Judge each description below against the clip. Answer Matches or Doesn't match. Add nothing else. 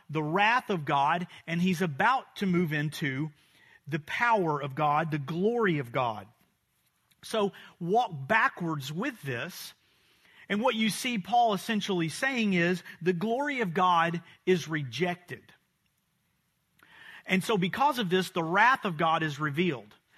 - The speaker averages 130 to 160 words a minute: Matches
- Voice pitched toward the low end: Doesn't match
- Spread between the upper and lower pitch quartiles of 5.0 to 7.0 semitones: Matches